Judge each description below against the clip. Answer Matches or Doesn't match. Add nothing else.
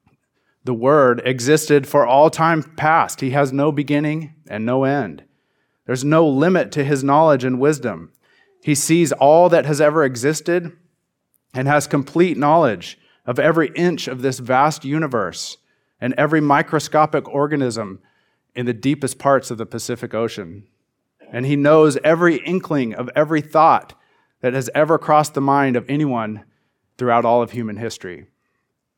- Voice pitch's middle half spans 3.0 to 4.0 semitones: Matches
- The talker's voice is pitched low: Doesn't match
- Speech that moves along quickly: Doesn't match